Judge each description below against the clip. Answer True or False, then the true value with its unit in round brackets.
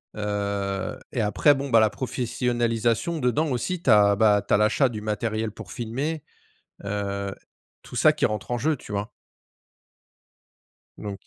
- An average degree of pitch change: True (3.3 semitones)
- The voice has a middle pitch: False (110 Hz)